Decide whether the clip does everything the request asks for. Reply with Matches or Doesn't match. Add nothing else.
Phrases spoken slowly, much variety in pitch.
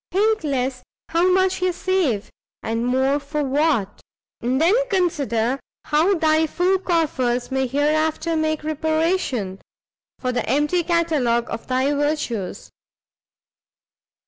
Doesn't match